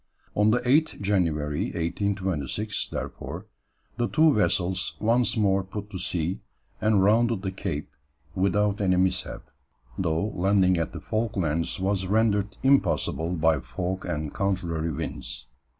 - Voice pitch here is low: Yes, very low, 95 Hz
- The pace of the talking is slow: Yes, slow, 130 wpm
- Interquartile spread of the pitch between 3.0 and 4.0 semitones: Yes, average, 3.4 semitones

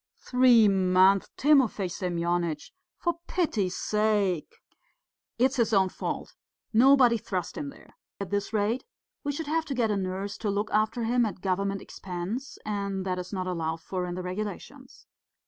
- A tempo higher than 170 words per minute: No, average, 160 wpm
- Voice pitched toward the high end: Yes, high, 205 Hz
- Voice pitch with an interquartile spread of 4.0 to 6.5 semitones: Yes, average, 4.4 semitones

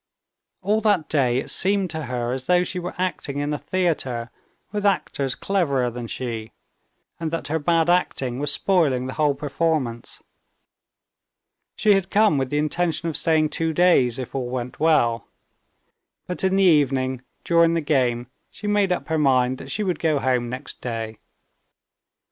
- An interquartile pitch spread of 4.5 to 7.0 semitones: Yes, wide, 5.6 semitones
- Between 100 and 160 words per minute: No, average, 170 wpm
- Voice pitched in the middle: Yes, medium, 150 Hz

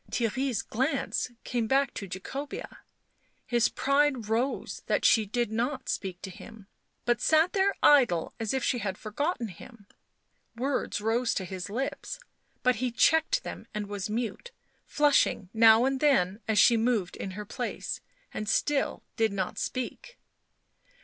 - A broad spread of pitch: No, average, 4.5 semitones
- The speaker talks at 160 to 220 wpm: No, average, 150 wpm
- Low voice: No, high, 235 Hz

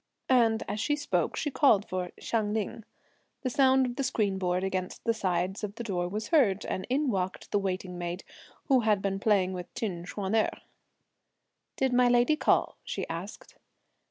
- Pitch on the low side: No, high, 210 Hz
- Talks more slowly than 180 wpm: No, average, 185 wpm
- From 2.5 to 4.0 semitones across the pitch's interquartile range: No, average, 4.6 semitones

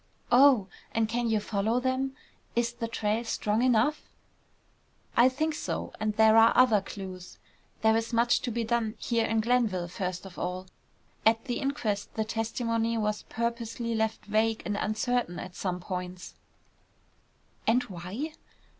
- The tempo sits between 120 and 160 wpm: Yes, average, 150 wpm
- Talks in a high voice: Yes, high, 225 Hz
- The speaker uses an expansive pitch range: No, narrow, 2.4 semitones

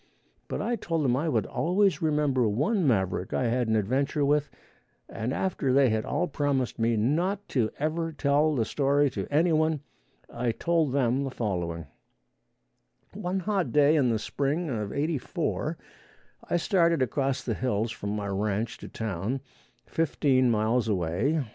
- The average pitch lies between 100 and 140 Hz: Yes, low, 135 Hz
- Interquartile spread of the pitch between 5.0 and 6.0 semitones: Yes, wide, 5.6 semitones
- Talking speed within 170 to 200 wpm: No, average, 160 wpm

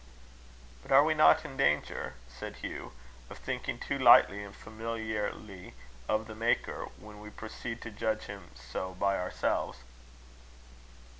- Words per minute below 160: Yes, average, 140 wpm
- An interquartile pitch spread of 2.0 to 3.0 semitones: Yes, narrow, 2.5 semitones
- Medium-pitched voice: No, low, 105 Hz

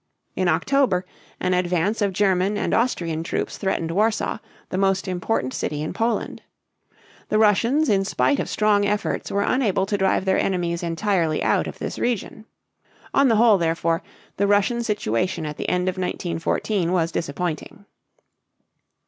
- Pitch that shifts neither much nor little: Yes, average, 3.6 semitones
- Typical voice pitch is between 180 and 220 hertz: Yes, high, 190 Hz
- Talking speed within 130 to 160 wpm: Yes, average, 155 wpm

